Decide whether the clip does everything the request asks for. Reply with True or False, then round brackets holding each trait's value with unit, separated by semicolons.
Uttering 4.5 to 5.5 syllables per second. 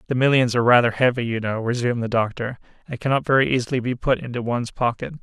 False (7.1 syllables/s)